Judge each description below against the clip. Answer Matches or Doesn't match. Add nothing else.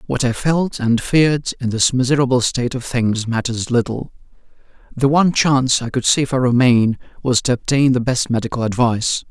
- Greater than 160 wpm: Matches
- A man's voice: Matches